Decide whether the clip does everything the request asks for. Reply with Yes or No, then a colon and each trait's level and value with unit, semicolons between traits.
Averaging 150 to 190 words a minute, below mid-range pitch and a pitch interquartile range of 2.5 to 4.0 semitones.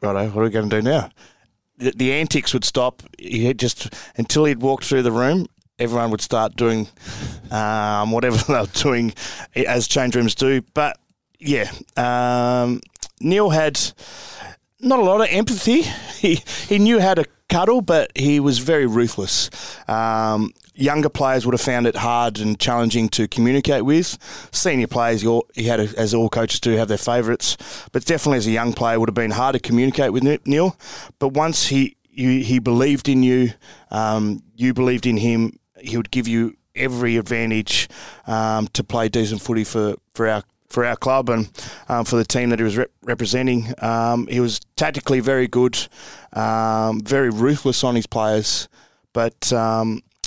Yes: average, 175 wpm; low, 120 Hz; average, 3.0 semitones